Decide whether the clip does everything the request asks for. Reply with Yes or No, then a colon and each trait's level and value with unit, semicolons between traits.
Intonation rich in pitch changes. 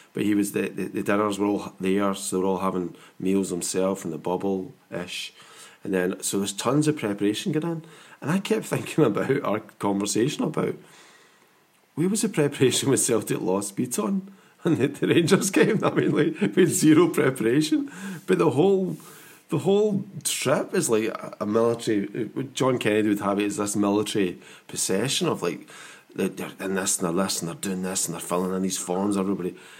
Yes: wide, 8.4 semitones